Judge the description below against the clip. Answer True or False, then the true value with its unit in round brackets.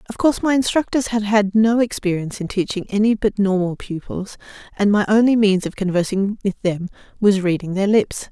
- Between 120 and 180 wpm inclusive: False (190 wpm)